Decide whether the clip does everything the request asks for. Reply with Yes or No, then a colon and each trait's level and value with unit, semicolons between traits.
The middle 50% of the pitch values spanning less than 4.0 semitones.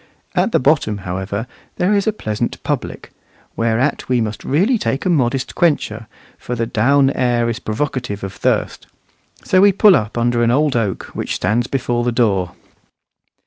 No: average, 4.7 semitones